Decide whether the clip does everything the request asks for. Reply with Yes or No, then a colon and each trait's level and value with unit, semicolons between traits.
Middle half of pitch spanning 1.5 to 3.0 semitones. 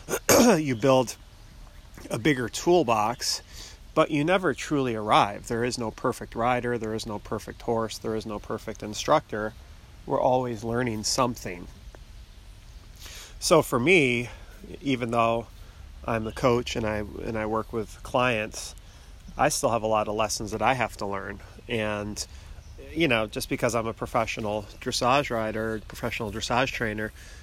Yes: narrow, 2.6 semitones